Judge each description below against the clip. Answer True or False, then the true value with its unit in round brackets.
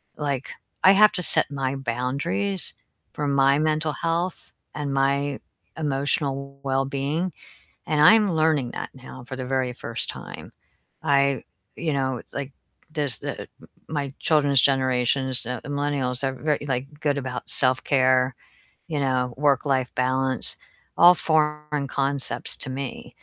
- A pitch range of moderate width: False (2.2 semitones)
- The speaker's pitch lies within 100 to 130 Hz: False (140 Hz)